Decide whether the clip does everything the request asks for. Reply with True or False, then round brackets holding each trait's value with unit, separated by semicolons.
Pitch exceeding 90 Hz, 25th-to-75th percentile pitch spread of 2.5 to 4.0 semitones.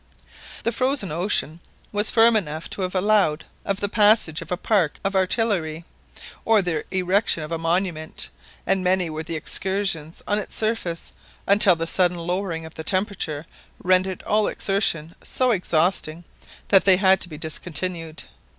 True (185 Hz; 3.6 semitones)